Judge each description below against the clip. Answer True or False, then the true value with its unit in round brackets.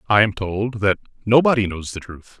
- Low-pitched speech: True (105 Hz)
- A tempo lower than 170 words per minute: False (200 wpm)